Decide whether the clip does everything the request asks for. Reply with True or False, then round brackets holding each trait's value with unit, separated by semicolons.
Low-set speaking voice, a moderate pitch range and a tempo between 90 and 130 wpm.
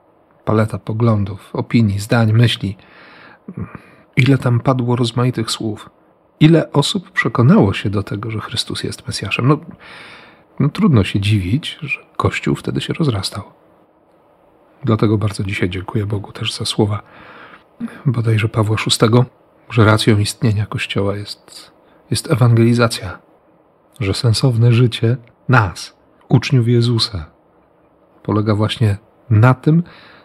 True (115 Hz; 3.1 semitones; 115 wpm)